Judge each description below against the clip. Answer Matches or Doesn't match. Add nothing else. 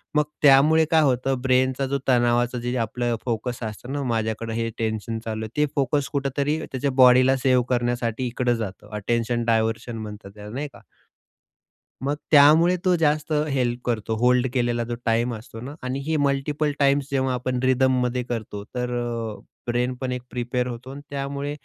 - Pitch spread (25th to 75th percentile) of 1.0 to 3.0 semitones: Matches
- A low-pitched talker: Matches